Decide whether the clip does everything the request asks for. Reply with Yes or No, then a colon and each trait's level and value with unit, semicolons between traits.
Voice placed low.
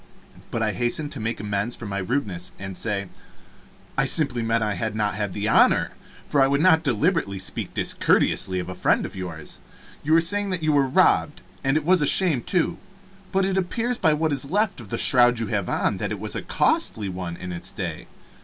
Yes: low, 120 Hz